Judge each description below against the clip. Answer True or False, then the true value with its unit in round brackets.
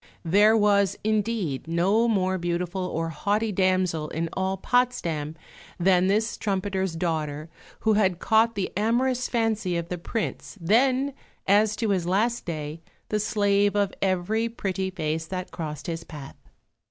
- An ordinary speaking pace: True (145 wpm)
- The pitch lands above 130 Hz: True (190 Hz)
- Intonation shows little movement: False (4.2 semitones)